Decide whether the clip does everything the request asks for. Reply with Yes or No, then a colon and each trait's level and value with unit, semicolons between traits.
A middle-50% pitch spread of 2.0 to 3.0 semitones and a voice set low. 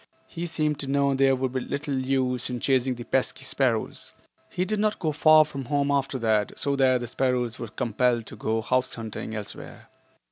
Yes: narrow, 2.6 semitones; low, 130 Hz